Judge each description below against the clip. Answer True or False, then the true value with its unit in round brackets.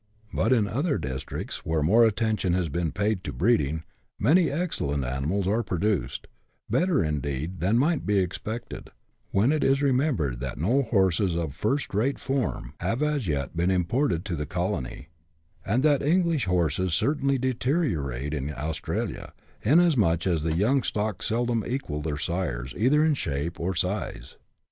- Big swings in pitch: True (8.7 semitones)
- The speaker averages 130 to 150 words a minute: False (160 wpm)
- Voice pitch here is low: True (95 Hz)